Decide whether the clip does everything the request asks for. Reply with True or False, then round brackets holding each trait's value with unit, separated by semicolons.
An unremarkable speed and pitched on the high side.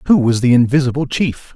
False (195 wpm; 130 Hz)